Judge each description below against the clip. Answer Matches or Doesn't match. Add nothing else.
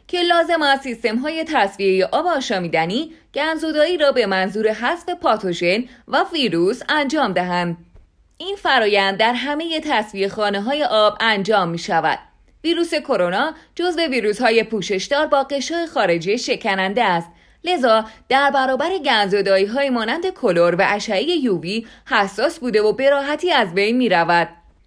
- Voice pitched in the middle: Doesn't match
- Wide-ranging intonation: Matches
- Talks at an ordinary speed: Matches